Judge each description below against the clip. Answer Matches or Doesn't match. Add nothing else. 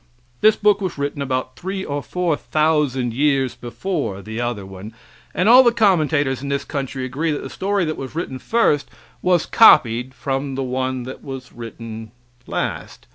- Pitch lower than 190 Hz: Matches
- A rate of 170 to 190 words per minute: Matches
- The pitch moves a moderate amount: Matches